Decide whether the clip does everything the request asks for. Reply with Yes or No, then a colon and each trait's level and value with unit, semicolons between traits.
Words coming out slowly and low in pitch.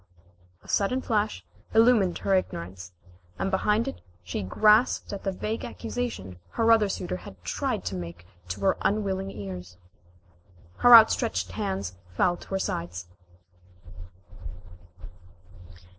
No: slow, 125 wpm; high, 190 Hz